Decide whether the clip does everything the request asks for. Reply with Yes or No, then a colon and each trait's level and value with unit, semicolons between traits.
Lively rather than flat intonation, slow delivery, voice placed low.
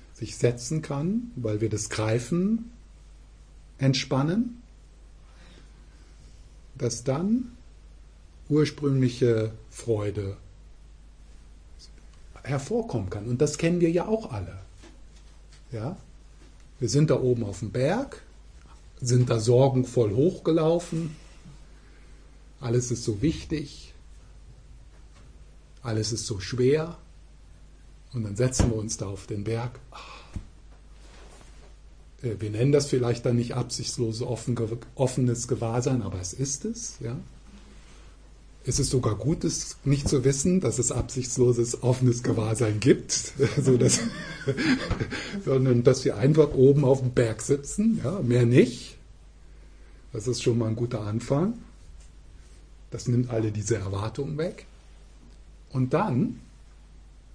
Yes: wide, 7.9 semitones; slow, 110 wpm; low, 120 Hz